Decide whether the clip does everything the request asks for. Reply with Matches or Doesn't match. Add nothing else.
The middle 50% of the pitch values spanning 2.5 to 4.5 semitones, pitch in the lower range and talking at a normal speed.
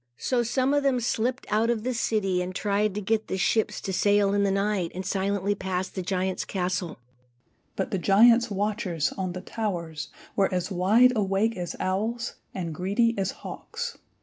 Doesn't match